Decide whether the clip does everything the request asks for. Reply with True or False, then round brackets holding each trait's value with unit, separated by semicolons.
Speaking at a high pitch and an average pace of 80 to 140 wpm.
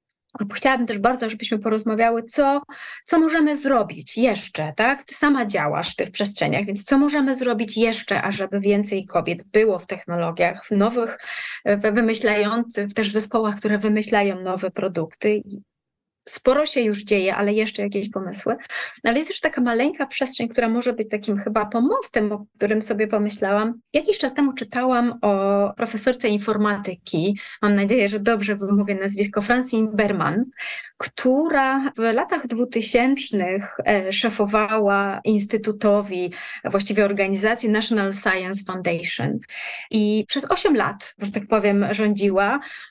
True (215 Hz; 135 wpm)